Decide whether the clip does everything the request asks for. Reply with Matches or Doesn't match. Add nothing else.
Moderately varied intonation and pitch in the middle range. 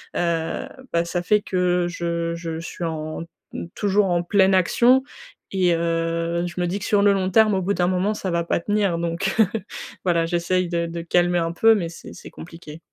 Doesn't match